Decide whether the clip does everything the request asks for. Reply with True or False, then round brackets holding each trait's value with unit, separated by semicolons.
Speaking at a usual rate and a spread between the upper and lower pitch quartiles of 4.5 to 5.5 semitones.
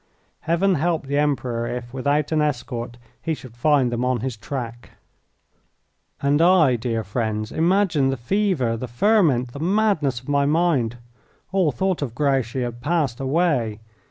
True (155 wpm; 5.1 semitones)